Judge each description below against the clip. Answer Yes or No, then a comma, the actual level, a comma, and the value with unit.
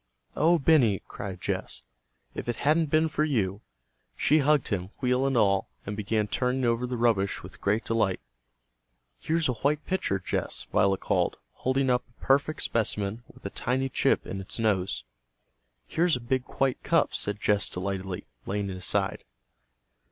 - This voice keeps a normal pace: Yes, average, 165 wpm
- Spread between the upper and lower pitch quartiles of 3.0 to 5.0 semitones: No, wide, 5.4 semitones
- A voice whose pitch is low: Yes, low, 115 Hz